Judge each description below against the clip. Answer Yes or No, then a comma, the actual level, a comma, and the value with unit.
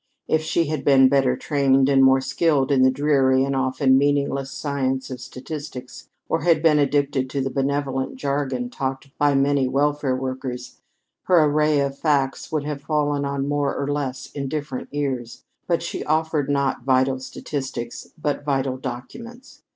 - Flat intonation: Yes, narrow, 1.8 semitones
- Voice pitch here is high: No, medium, 140 Hz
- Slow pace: No, average, 160 wpm